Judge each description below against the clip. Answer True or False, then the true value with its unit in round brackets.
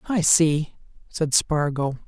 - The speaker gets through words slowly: True (115 wpm)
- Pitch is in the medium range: True (155 Hz)